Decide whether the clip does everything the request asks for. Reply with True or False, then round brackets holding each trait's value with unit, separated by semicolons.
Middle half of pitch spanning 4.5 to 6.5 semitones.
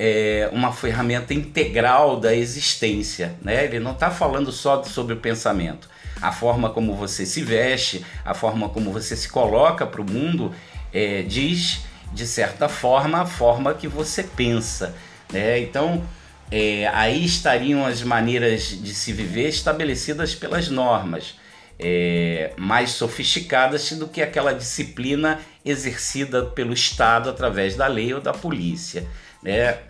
True (4.9 semitones)